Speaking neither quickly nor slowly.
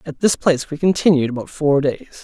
No: fast, 215 wpm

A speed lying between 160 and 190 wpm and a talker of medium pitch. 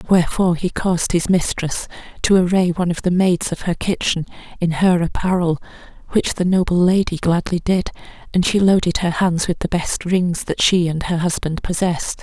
Yes: average, 185 wpm; medium, 175 Hz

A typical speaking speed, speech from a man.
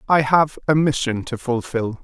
Yes: average, 175 wpm; male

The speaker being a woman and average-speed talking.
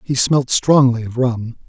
No: male; average, 180 wpm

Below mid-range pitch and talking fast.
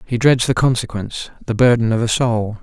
No: low, 115 Hz; average, 185 wpm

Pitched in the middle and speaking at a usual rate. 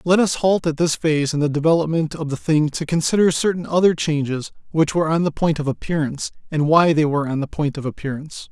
No: medium, 155 Hz; fast, 230 wpm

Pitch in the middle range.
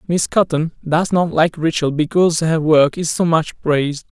Yes: medium, 160 Hz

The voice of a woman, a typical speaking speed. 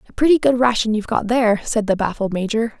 No: female; fast, 255 wpm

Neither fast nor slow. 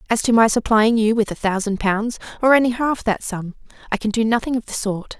No: fast, 245 wpm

